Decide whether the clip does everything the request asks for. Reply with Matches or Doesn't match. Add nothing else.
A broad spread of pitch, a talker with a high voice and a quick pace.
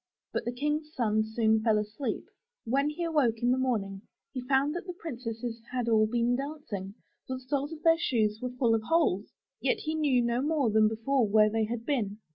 Doesn't match